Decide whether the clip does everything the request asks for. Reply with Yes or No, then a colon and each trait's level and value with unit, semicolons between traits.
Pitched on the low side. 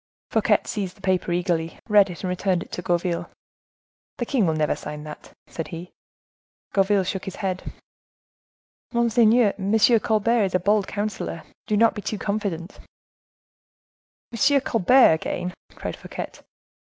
No: high, 195 Hz